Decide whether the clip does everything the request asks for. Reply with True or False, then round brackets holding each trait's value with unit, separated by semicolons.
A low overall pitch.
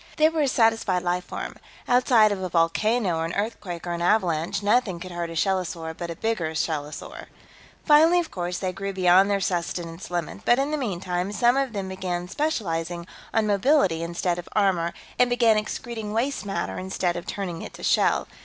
False (190 Hz)